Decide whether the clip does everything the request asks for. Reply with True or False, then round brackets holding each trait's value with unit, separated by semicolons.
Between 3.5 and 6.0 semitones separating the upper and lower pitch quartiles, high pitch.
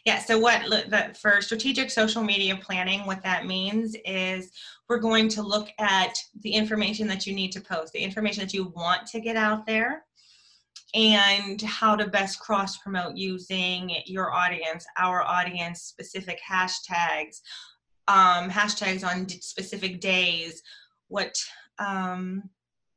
False (2.7 semitones; 195 Hz)